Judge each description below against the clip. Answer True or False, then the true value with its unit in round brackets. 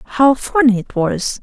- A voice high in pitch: True (240 Hz)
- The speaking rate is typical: True (170 wpm)